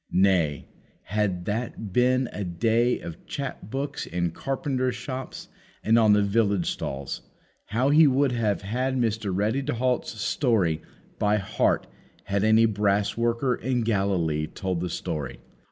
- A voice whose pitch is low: Yes, low, 110 Hz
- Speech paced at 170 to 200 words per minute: No, average, 145 wpm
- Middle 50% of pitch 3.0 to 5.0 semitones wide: Yes, average, 4.4 semitones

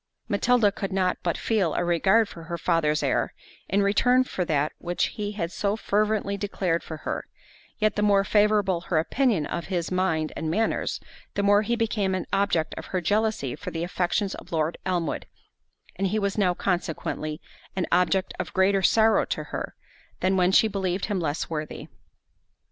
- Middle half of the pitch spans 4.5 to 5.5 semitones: No, average, 3.3 semitones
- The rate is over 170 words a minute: Yes, average, 180 wpm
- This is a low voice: No, high, 190 Hz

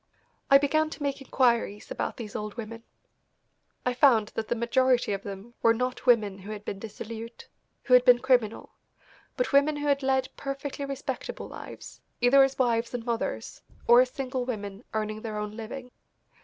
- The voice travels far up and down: No, average, 3.5 semitones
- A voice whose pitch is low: No, high, 240 Hz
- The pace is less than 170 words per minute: No, average, 175 wpm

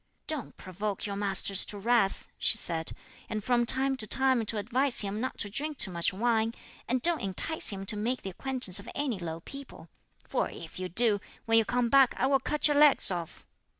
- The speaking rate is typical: No, fast, 210 wpm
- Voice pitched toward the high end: Yes, high, 225 Hz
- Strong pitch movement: No, average, 5.0 semitones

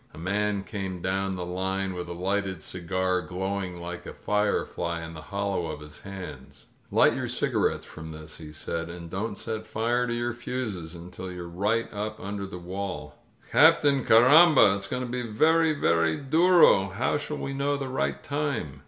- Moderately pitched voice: No, very low, 95 Hz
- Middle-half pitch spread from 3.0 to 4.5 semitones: No, average, 5.2 semitones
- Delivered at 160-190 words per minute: Yes, average, 180 wpm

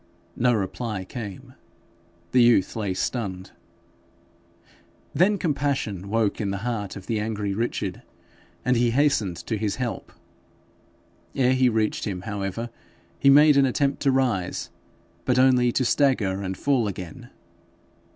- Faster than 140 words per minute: No, slow, 135 wpm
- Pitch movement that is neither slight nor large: Yes, average, 4.5 semitones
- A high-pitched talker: No, low, 115 Hz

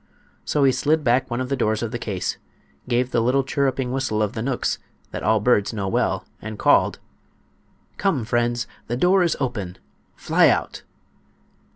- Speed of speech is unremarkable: Yes, average, 170 wpm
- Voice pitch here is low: Yes, low, 120 Hz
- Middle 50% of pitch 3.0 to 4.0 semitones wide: Yes, average, 3.5 semitones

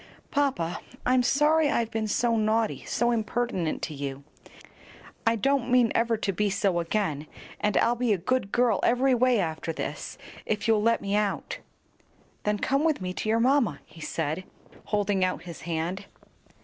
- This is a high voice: Yes, high, 215 Hz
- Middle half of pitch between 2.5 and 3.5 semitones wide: No, average, 4.8 semitones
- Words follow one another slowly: No, average, 170 wpm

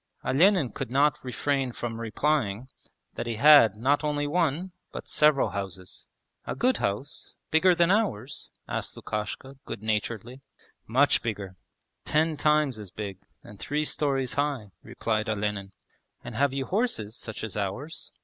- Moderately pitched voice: No, low, 130 Hz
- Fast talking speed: No, average, 145 wpm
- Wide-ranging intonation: Yes, wide, 5.7 semitones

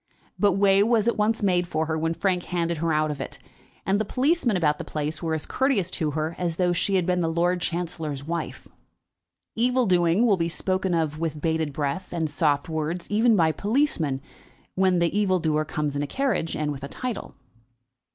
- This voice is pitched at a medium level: Yes, medium, 170 Hz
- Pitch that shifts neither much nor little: Yes, average, 3.9 semitones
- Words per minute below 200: No, fast, 205 wpm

